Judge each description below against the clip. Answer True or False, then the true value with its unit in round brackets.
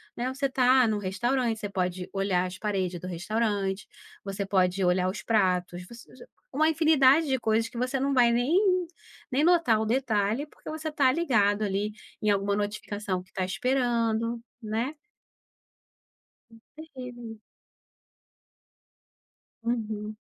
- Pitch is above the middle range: True (225 Hz)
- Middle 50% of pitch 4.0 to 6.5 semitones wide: True (4.7 semitones)